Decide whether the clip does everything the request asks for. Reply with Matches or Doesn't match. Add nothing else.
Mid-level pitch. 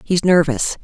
Matches